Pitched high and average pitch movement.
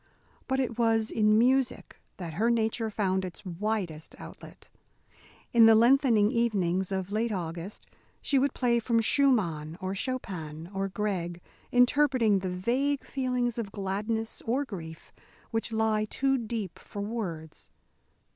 Yes: high, 220 Hz; average, 4.1 semitones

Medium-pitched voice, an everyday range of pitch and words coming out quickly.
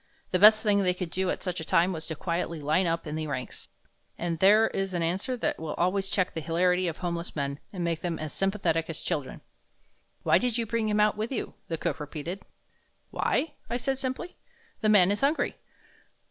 Yes: medium, 180 Hz; average, 4.3 semitones; fast, 215 wpm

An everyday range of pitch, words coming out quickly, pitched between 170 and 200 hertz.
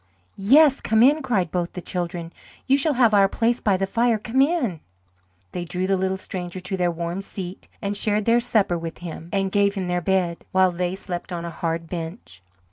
Yes: average, 3.7 semitones; fast, 210 wpm; high, 190 Hz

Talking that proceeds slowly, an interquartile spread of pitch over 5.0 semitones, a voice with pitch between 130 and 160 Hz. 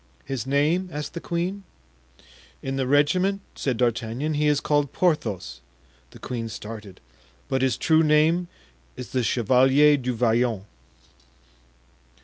No: slow, 130 wpm; average, 4.1 semitones; low, 135 Hz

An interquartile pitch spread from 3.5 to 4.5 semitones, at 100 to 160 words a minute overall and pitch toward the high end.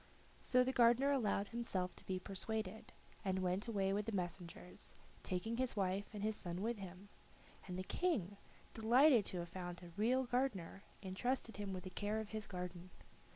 No: average, 4.0 semitones; average, 180 wpm; high, 205 Hz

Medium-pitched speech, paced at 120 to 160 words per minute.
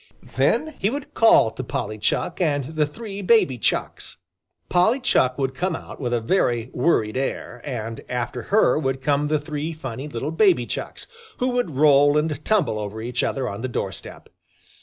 No: medium, 145 Hz; average, 180 wpm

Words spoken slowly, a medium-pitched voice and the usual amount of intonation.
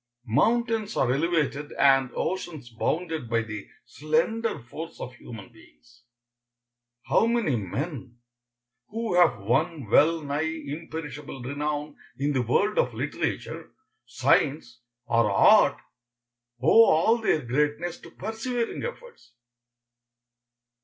No: slow, 110 wpm; medium, 150 Hz; wide, 6.3 semitones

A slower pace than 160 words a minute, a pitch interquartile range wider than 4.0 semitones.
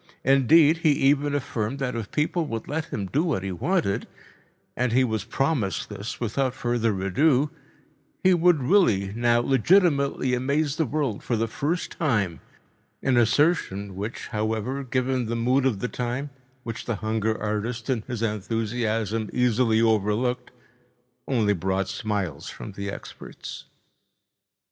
Yes: average, 140 wpm; average, 4.5 semitones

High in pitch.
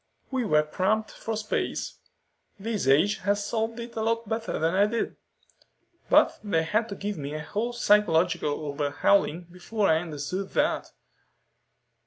Yes: high, 200 Hz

